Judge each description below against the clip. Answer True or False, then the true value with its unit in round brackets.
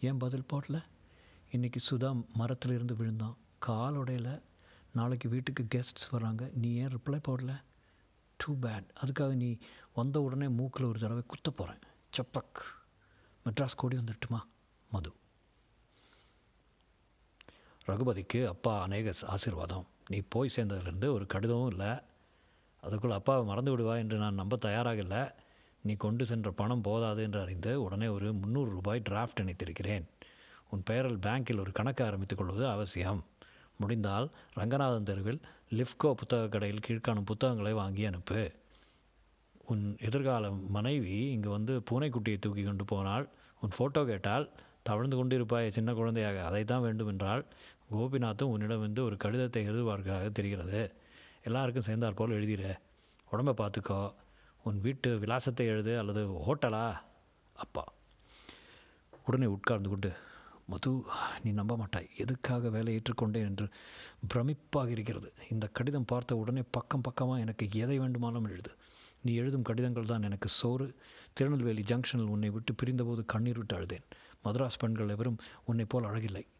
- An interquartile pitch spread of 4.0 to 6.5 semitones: False (3.4 semitones)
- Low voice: True (115 Hz)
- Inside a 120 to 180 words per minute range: True (130 wpm)